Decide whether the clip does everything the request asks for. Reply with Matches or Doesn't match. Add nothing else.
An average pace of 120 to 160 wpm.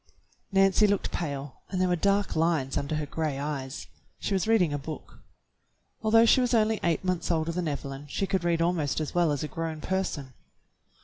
Doesn't match